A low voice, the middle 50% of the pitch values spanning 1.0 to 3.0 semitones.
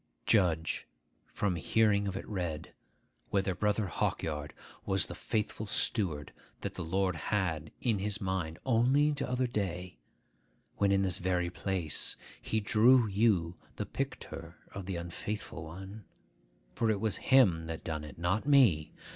No: very low, 95 Hz; average, 4.0 semitones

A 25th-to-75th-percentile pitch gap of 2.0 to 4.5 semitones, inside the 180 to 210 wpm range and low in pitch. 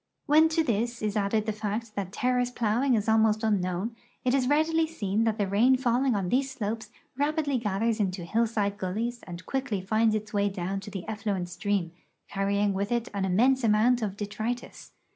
No: average, 3.4 semitones; average, 190 wpm; high, 215 Hz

